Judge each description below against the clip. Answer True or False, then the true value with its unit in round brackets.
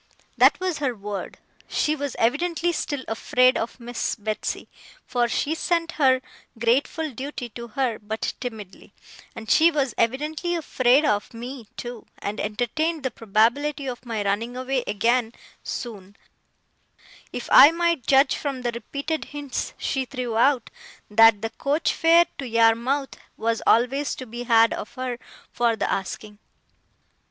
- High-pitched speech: True (250 Hz)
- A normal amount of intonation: True (4.0 semitones)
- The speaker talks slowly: False (145 wpm)